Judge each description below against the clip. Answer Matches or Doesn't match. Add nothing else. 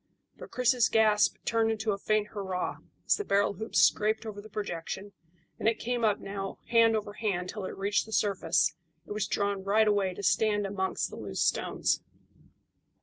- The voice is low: Doesn't match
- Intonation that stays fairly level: Matches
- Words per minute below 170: Doesn't match